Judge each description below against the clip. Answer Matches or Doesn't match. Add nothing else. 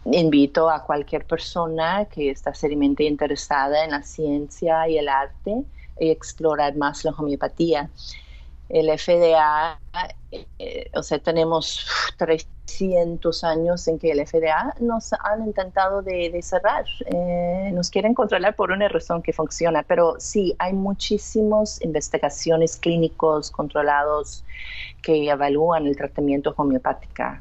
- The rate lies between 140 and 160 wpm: Doesn't match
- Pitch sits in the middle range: Matches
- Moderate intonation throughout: Matches